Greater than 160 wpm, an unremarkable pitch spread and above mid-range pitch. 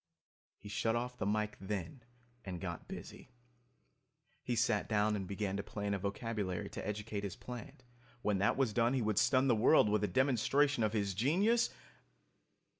No: average, 175 wpm; average, 3.5 semitones; low, 105 Hz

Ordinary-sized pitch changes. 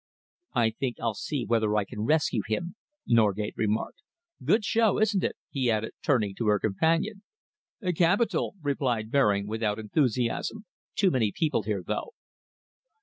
No: wide, 7.1 semitones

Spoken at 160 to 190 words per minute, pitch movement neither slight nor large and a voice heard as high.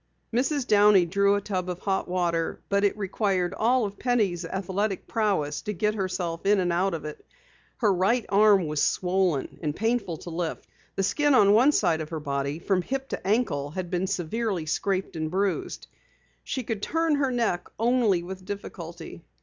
Yes: average, 180 wpm; average, 3.7 semitones; high, 195 Hz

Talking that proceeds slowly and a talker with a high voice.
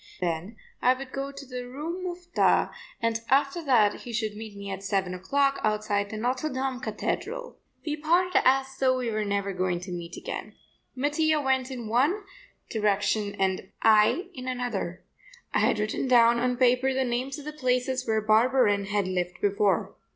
No: average, 175 wpm; high, 245 Hz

